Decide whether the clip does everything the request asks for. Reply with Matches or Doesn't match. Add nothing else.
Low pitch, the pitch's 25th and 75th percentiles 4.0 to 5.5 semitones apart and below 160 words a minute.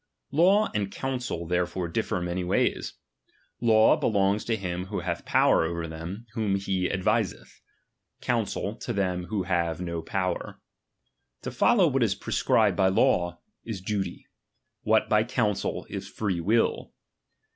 Doesn't match